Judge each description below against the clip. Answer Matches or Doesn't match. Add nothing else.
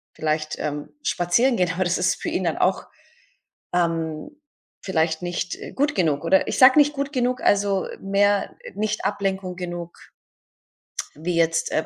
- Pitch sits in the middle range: Matches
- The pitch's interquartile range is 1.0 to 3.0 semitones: Doesn't match